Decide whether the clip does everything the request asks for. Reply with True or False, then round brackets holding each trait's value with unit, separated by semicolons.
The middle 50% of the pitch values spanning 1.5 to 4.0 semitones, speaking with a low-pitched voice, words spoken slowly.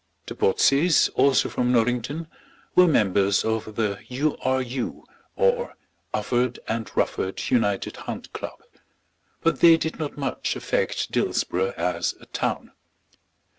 False (5.4 semitones; 125 Hz; 130 wpm)